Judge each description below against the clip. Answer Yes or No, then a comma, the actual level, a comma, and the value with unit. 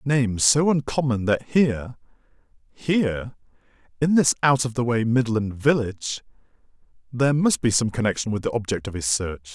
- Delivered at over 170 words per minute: No, average, 150 wpm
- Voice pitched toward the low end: Yes, low, 120 Hz